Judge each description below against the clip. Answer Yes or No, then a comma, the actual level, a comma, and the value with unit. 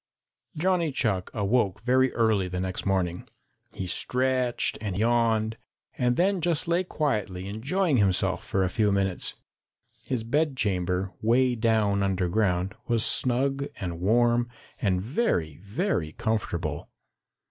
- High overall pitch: No, low, 110 Hz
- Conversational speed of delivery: No, slow, 125 wpm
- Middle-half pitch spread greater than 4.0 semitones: Yes, average, 5.3 semitones